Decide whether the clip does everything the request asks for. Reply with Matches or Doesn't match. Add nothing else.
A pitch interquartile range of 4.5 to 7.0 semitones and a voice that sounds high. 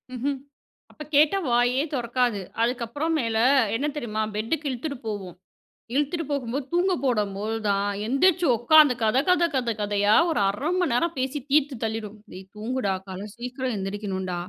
Matches